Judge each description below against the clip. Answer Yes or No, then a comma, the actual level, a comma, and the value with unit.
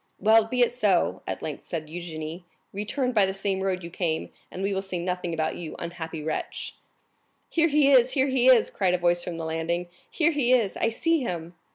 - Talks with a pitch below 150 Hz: No, high, 190 Hz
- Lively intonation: Yes, wide, 6.1 semitones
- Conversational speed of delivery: No, fast, 215 wpm